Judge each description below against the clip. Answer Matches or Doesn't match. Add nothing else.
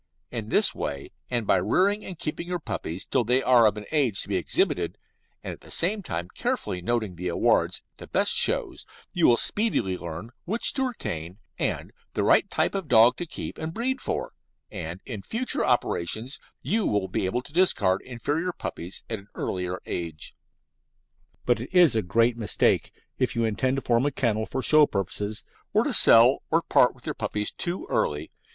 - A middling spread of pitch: Doesn't match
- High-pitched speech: Doesn't match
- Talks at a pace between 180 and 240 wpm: Matches